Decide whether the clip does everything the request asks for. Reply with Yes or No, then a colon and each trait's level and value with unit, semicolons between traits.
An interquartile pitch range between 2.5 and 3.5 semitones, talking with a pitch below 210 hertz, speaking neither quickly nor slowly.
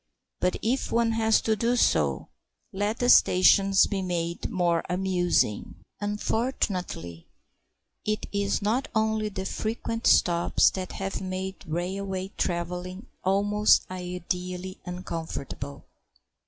No: average, 2.9 semitones; high, 190 Hz; slow, 110 wpm